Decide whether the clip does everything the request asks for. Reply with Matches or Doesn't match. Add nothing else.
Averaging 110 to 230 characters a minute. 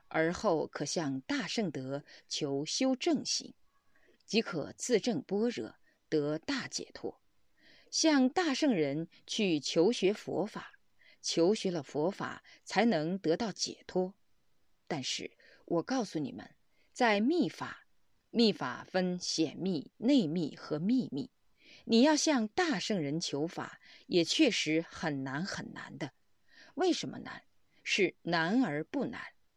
Matches